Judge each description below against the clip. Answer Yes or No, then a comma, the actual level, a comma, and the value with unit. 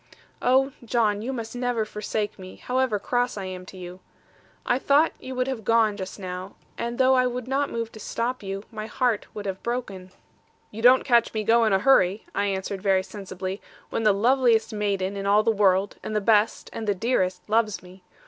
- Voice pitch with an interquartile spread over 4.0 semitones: No, average, 3.7 semitones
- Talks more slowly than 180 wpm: No, fast, 205 wpm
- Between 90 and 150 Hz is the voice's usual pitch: No, high, 215 Hz